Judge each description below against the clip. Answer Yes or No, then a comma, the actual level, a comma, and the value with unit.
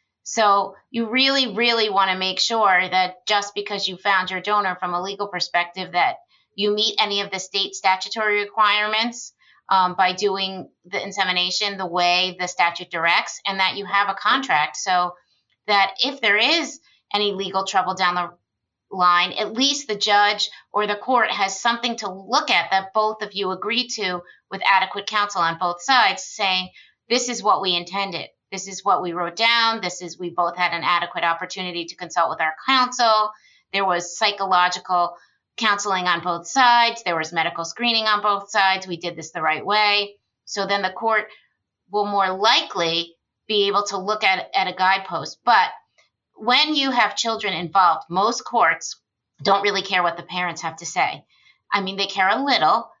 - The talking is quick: No, average, 185 wpm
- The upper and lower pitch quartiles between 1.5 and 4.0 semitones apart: Yes, average, 3.0 semitones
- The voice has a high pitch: Yes, high, 195 Hz